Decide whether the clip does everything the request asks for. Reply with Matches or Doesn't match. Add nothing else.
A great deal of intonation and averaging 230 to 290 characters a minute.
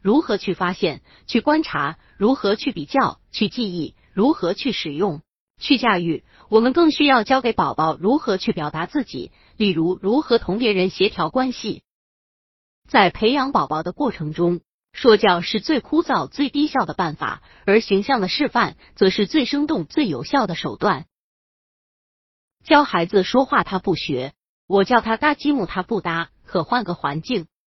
Matches